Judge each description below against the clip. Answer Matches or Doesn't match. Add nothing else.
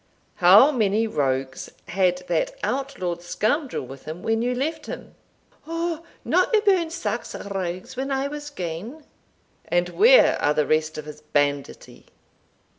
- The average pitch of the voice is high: Matches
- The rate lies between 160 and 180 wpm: Doesn't match